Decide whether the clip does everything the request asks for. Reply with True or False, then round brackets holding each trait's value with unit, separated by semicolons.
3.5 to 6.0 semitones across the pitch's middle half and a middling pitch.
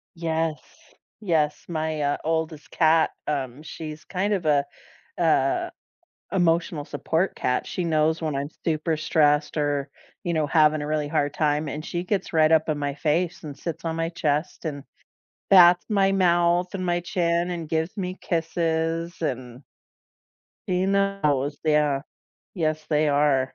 False (2.6 semitones; 160 Hz)